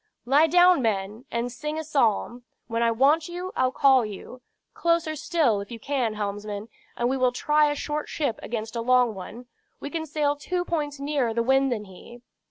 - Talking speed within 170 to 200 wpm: Yes, average, 195 wpm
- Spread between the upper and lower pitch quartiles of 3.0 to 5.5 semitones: Yes, average, 4.7 semitones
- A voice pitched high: Yes, very high, 255 Hz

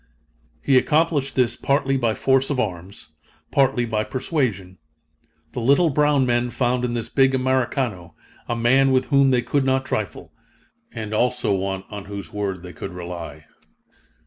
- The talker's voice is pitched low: Yes, low, 120 Hz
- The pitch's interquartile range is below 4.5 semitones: No, average, 5.0 semitones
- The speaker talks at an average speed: Yes, average, 155 wpm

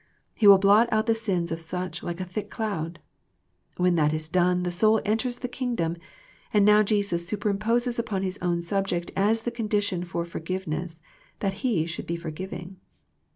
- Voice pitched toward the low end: No, high, 190 Hz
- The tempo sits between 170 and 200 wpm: Yes, average, 175 wpm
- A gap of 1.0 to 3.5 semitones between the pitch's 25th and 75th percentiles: No, average, 3.9 semitones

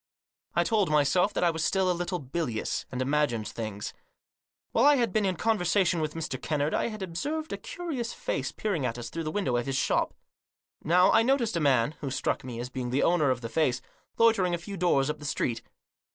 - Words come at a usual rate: No, fast, 225 wpm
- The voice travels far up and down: Yes, wide, 6.9 semitones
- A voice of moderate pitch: Yes, medium, 160 Hz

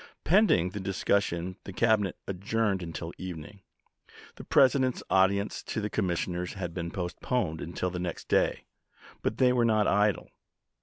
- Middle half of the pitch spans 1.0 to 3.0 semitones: No, average, 3.4 semitones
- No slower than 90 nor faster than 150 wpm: Yes, average, 145 wpm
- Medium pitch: No, very low, 95 Hz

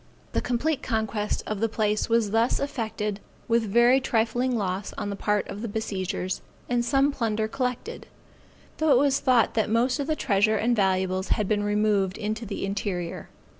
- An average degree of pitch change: Yes, average, 3.0 semitones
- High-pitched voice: Yes, high, 220 Hz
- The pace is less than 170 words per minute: No, average, 175 wpm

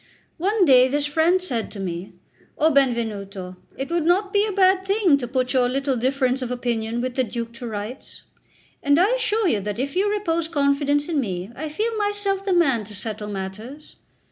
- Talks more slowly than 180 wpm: No, average, 195 wpm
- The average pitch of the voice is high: Yes, very high, 275 Hz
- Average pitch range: No, wide, 7.2 semitones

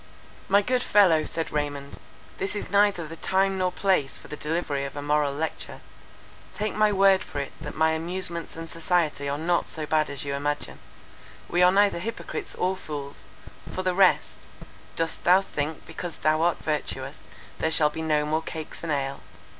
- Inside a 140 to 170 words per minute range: No, average, 185 wpm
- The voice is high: No, medium, 160 Hz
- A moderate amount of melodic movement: Yes, average, 3.8 semitones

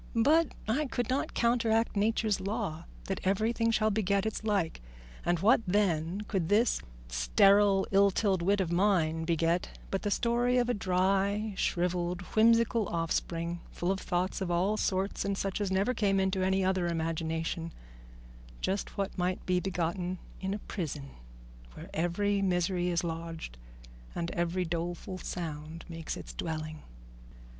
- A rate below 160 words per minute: Yes, average, 150 wpm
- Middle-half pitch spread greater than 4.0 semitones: No, average, 3.3 semitones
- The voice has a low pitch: No, high, 190 Hz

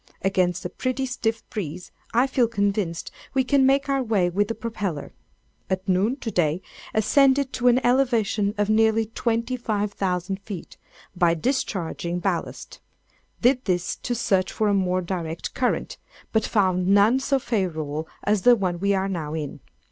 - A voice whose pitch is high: Yes, high, 205 Hz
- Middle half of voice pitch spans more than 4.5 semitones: Yes, average, 4.9 semitones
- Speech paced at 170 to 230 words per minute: No, average, 155 wpm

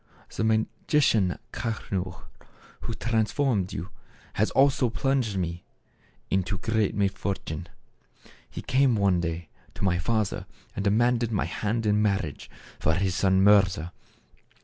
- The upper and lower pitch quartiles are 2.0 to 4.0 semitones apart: Yes, average, 3.4 semitones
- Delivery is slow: Yes, slow, 125 wpm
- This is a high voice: No, low, 100 Hz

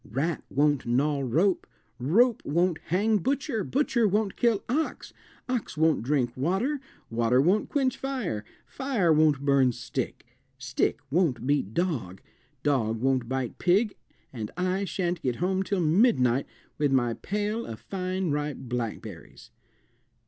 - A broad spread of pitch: Yes, wide, 7.5 semitones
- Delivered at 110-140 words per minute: Yes, slow, 135 wpm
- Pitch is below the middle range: No, medium, 160 Hz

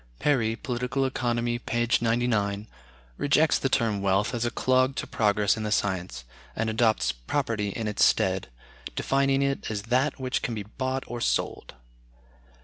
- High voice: No, low, 120 Hz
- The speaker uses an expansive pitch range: No, average, 3.5 semitones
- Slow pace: No, average, 155 wpm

